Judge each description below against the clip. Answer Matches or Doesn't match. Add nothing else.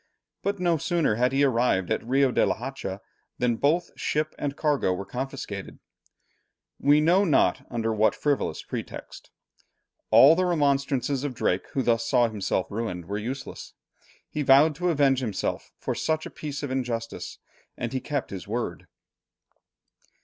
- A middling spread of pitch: Matches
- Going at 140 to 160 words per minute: Matches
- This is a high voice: Doesn't match